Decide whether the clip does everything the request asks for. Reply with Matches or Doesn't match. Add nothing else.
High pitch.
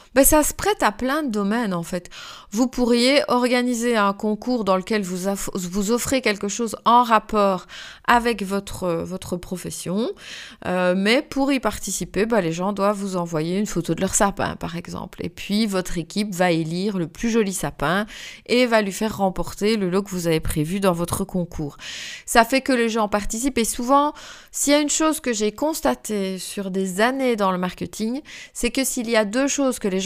Matches